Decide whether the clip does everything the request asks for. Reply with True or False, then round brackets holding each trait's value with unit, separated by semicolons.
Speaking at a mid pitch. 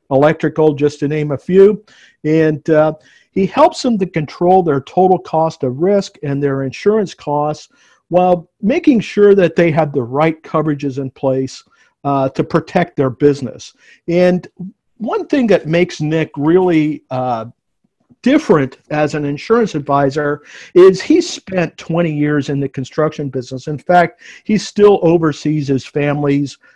True (155 Hz)